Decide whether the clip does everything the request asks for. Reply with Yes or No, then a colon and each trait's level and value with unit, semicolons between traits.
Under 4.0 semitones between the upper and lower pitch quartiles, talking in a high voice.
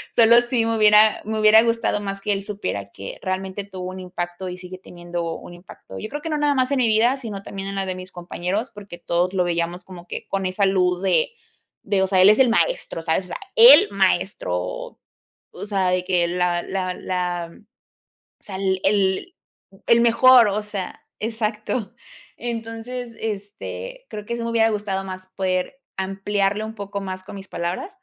Yes: average, 3.5 semitones; high, 195 Hz